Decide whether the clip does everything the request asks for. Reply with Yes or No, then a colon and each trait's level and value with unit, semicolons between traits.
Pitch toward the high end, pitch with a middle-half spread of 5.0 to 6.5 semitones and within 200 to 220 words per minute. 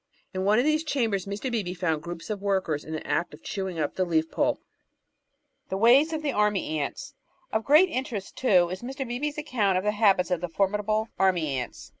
Yes: high, 200 Hz; wide, 5.5 semitones; fast, 205 wpm